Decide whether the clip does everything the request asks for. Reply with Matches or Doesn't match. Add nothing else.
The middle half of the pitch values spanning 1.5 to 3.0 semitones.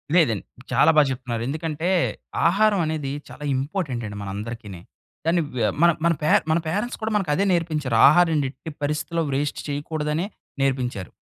Doesn't match